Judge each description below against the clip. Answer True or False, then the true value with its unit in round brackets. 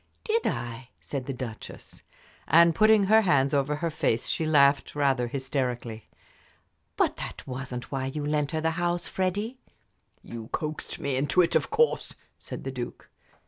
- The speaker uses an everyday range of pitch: True (4.7 semitones)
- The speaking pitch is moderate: True (145 Hz)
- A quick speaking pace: False (160 wpm)